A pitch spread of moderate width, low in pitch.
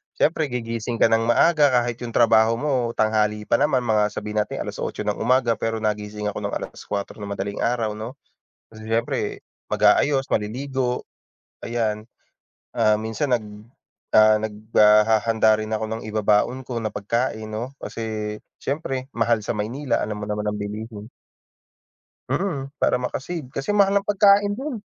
Yes: average, 3.3 semitones; low, 115 Hz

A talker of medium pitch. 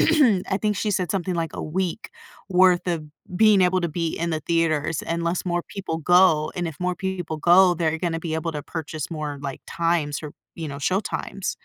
Yes: medium, 170 Hz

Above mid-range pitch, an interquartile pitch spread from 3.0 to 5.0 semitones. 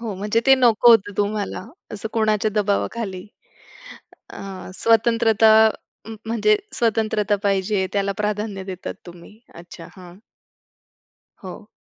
No: high, 210 Hz; narrow, 2.4 semitones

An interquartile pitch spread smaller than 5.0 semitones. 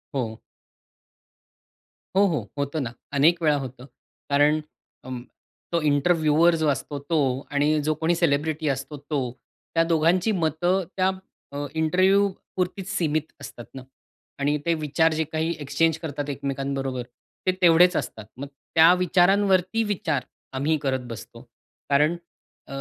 Yes: average, 3.3 semitones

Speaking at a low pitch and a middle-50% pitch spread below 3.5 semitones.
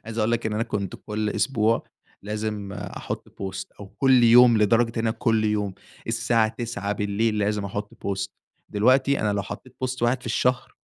Yes: low, 110 Hz; narrow, 2.4 semitones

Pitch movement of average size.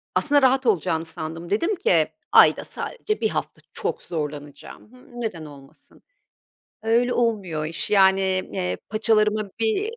No: wide, 7.3 semitones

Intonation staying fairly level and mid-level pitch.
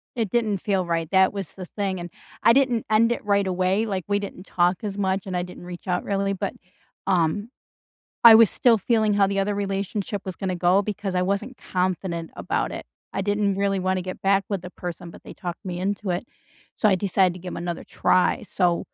No: narrow, 2.1 semitones; high, 195 Hz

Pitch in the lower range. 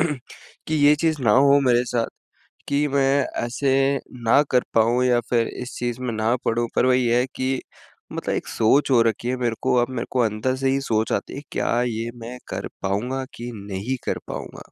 Yes: low, 125 Hz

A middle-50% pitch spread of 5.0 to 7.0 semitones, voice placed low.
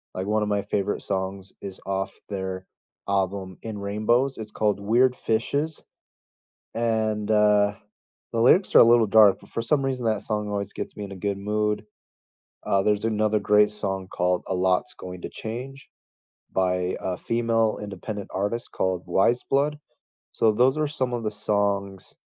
No: average, 2.8 semitones; low, 105 Hz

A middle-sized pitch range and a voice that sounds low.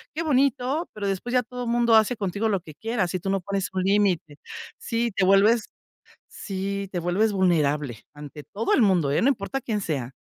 No: average, 4.5 semitones; high, 200 Hz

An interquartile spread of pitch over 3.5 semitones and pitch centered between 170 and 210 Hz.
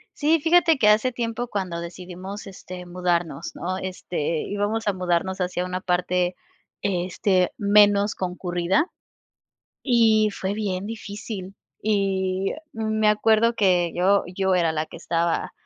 No: average, 2.9 semitones; high, 190 Hz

